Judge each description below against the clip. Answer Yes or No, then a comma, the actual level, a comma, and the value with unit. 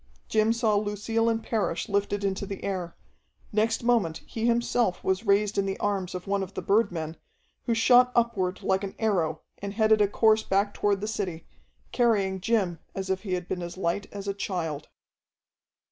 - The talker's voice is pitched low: No, high, 200 Hz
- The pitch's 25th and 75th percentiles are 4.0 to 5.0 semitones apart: No, average, 2.7 semitones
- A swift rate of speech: No, average, 185 wpm